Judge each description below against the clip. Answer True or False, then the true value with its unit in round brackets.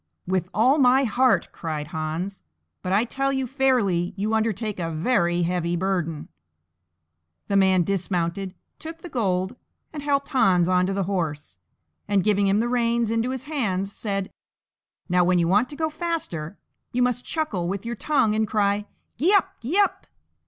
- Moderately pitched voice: False (200 Hz)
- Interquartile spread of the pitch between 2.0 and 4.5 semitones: False (5.6 semitones)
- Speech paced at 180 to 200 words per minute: False (170 wpm)